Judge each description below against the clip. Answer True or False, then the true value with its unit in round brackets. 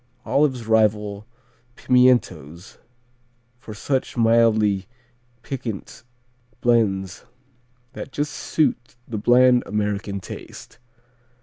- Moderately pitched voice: False (115 Hz)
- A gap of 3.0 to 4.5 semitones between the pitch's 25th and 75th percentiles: True (3.5 semitones)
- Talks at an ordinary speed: False (80 wpm)